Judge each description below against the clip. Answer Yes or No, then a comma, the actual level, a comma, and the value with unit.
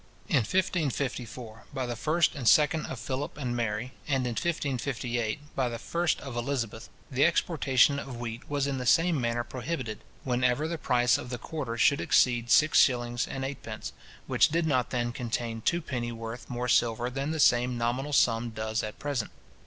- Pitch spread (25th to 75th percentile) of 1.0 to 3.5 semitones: Yes, average, 3.1 semitones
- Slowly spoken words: No, average, 180 wpm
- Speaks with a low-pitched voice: Yes, low, 125 Hz